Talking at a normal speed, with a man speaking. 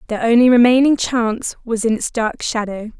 No: average, 180 wpm; female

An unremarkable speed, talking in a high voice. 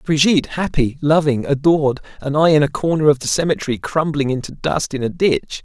No: average, 190 wpm; medium, 145 Hz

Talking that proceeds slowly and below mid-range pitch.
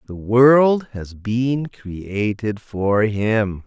Yes: slow, 115 wpm; low, 110 Hz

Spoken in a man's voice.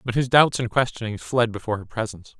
Yes: male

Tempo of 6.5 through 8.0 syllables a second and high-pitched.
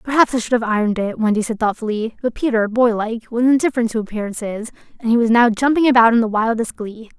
Yes: 6.6 syllables/s; high, 230 Hz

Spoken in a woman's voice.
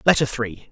No: male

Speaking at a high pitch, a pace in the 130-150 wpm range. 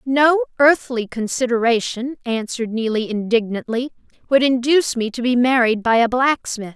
Yes: high, 245 Hz; slow, 135 wpm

